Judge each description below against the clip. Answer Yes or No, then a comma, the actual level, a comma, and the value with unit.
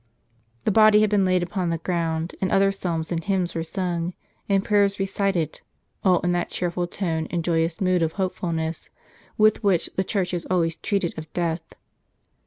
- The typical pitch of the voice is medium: Yes, medium, 180 Hz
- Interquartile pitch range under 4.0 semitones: Yes, average, 2.8 semitones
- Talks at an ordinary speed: Yes, average, 180 wpm